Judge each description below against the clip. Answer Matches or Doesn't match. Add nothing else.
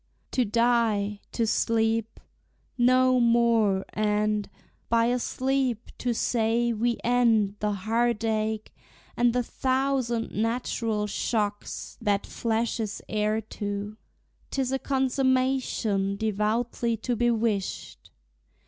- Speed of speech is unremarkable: Doesn't match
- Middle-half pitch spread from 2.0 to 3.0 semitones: Matches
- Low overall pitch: Doesn't match